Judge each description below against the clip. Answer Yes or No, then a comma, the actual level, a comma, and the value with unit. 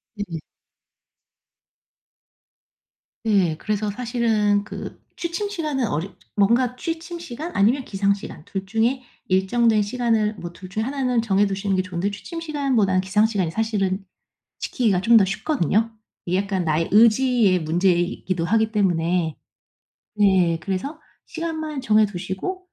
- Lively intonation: No, average, 4.6 semitones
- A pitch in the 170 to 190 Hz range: No, high, 210 Hz